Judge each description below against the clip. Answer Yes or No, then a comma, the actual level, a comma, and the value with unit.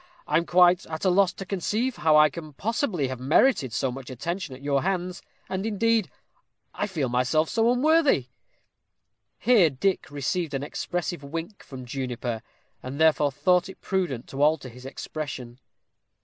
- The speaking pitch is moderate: Yes, medium, 160 Hz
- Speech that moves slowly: No, average, 165 wpm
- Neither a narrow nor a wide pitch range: No, wide, 6.0 semitones